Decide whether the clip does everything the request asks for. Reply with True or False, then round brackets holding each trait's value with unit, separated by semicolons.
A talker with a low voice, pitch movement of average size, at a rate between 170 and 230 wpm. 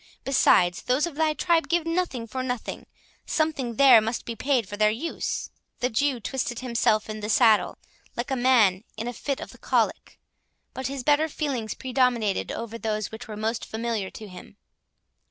False (245 Hz; 4.0 semitones; 180 wpm)